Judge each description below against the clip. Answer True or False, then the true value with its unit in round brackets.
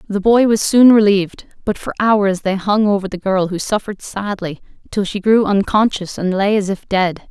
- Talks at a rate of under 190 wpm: False (205 wpm)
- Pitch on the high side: True (200 Hz)